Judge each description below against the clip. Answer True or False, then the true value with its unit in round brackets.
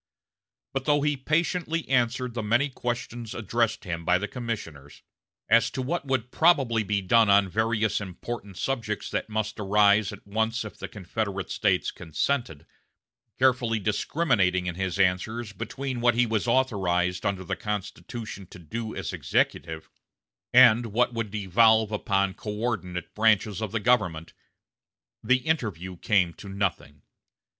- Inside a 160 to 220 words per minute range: False (145 wpm)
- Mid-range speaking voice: False (110 Hz)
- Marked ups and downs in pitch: False (4.0 semitones)